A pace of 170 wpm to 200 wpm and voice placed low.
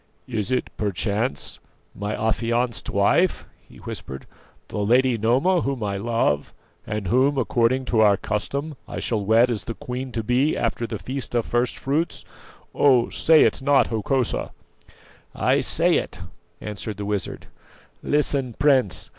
No: average, 145 wpm; low, 120 Hz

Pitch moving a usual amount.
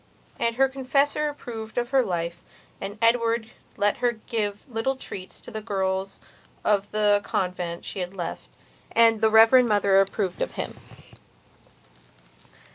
Yes: average, 3.5 semitones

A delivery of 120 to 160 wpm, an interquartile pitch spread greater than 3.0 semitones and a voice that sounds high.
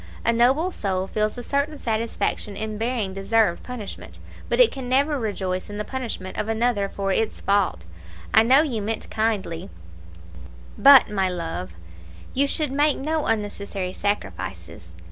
Yes: average, 150 wpm; average, 4.7 semitones; high, 220 Hz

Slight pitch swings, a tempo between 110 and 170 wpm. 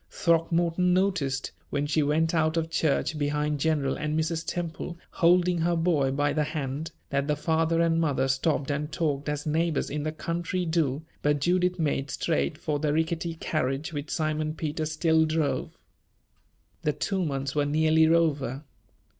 Yes: narrow, 2.2 semitones; average, 165 wpm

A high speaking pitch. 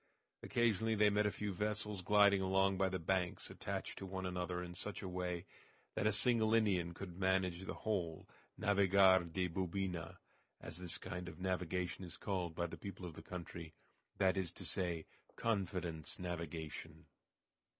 No: very low, 95 Hz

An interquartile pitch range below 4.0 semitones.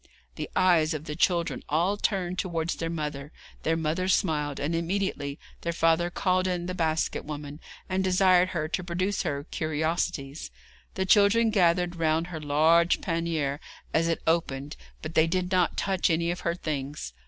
Yes: average, 2.8 semitones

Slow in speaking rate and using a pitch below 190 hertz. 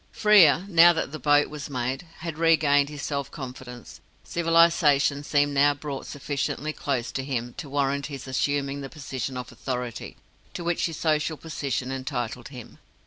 No: average, 160 wpm; medium, 140 Hz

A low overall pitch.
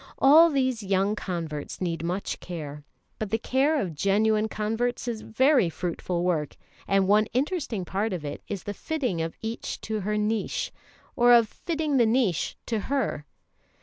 No: high, 215 Hz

